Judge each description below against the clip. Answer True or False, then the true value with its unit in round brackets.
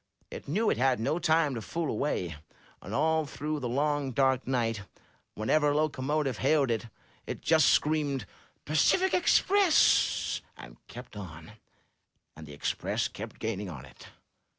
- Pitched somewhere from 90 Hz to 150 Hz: True (135 Hz)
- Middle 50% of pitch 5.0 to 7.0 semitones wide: True (5.5 semitones)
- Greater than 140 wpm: True (150 wpm)